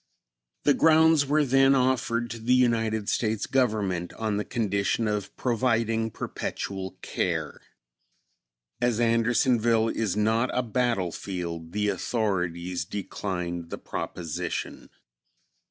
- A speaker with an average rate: No, slow, 105 wpm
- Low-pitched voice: Yes, low, 110 Hz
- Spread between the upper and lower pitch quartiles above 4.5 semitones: No, average, 4.1 semitones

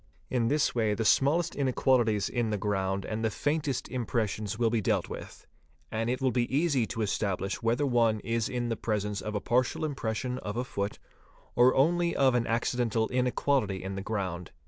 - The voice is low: Yes, low, 115 Hz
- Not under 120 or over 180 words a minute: No, average, 190 wpm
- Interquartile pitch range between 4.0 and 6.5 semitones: No, average, 3.3 semitones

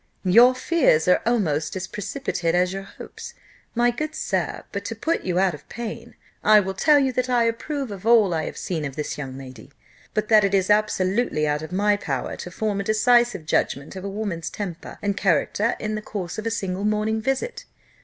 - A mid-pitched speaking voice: No, high, 205 Hz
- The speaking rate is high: Yes, fast, 210 wpm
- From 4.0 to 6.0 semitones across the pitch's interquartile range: Yes, average, 4.4 semitones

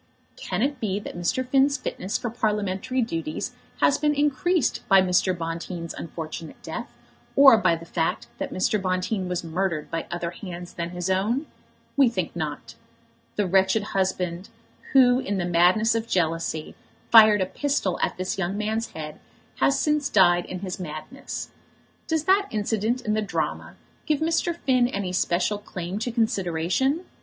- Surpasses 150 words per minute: Yes, average, 160 wpm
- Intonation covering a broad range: Yes, wide, 5.9 semitones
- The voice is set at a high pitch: Yes, high, 195 Hz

